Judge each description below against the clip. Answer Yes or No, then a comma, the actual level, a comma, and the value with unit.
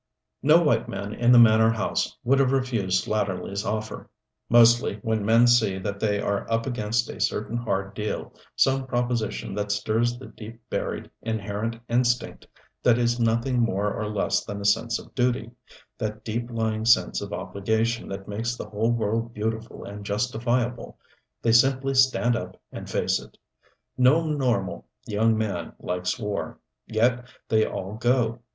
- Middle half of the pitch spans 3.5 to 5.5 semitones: No, narrow, 2.4 semitones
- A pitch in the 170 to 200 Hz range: No, low, 115 Hz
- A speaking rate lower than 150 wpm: No, average, 160 wpm